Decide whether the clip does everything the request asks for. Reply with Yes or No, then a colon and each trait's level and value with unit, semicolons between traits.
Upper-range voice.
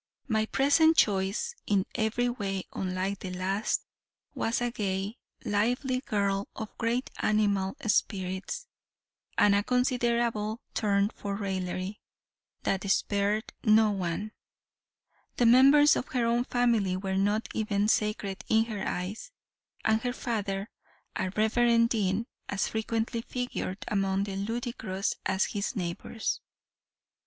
Yes: high, 210 Hz